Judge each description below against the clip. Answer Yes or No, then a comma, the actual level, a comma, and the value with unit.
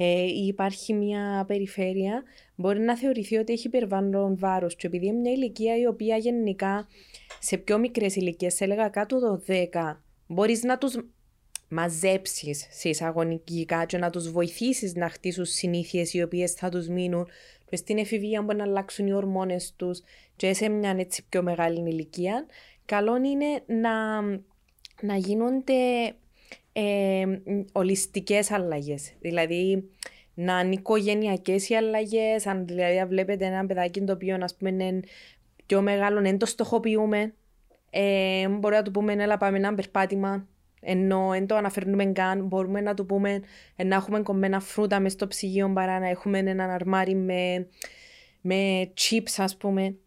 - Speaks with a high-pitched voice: Yes, high, 195 Hz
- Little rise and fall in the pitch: Yes, narrow, 2.3 semitones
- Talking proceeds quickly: No, average, 155 wpm